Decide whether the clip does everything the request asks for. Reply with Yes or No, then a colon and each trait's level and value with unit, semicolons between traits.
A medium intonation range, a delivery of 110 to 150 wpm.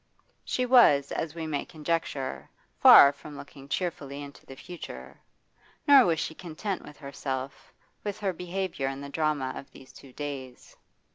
No: average, 3.8 semitones; average, 160 wpm